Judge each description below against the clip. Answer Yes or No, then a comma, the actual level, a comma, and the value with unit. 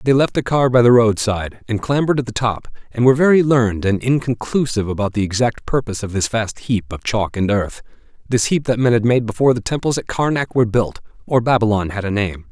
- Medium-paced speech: No, fast, 230 wpm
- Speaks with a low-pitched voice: Yes, low, 115 Hz